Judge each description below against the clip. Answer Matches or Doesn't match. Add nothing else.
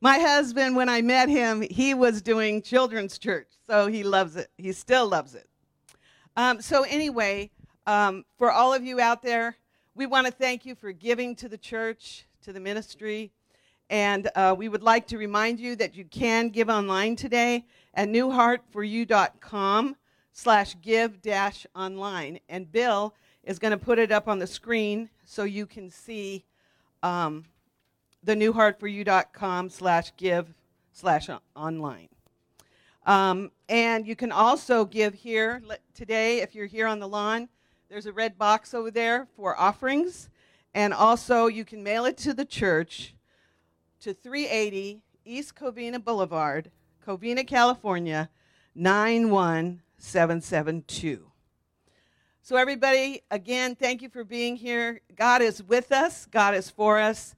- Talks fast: Doesn't match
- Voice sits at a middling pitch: Doesn't match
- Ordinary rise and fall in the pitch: Matches